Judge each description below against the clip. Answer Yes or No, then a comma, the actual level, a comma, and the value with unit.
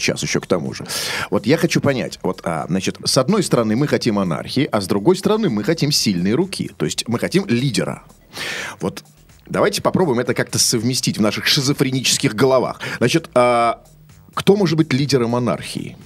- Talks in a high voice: No, low, 135 Hz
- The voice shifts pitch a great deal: Yes, wide, 5.7 semitones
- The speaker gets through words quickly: Yes, fast, 180 wpm